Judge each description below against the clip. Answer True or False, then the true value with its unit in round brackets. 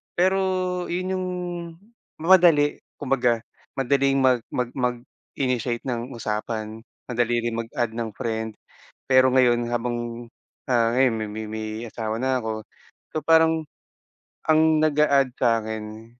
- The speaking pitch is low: True (120 Hz)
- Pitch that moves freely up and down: False (3.4 semitones)